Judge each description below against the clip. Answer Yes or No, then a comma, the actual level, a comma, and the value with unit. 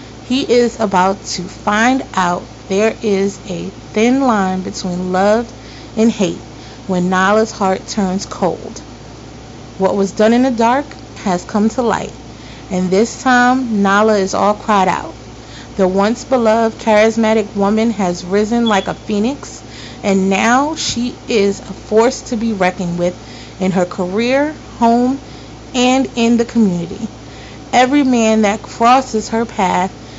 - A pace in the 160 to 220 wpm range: No, average, 145 wpm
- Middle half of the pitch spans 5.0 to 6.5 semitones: No, average, 4.0 semitones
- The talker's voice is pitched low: No, high, 210 Hz